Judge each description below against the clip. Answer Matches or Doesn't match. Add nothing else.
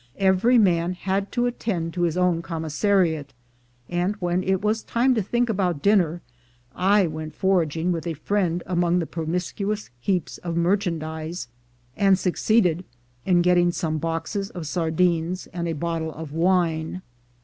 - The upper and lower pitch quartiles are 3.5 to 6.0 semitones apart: Doesn't match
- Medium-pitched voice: Matches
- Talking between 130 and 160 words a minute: Matches